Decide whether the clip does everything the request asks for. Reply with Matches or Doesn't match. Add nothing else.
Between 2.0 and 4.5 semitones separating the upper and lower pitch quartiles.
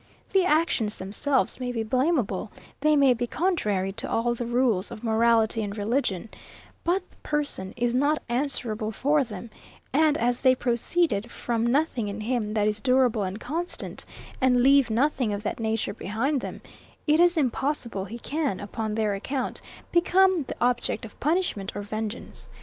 Doesn't match